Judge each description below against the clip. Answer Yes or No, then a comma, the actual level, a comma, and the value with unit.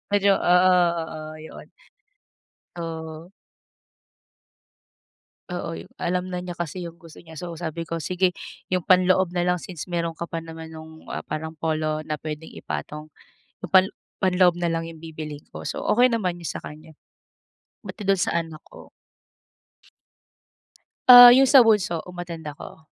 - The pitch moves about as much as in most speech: No, narrow, 2.2 semitones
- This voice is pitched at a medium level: Yes, medium, 170 Hz